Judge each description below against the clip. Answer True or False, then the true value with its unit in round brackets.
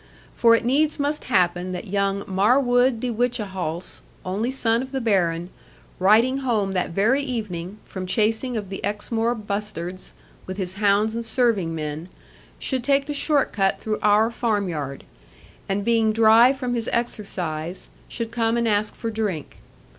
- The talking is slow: False (155 wpm)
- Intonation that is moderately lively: True (4.0 semitones)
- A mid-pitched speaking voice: False (215 Hz)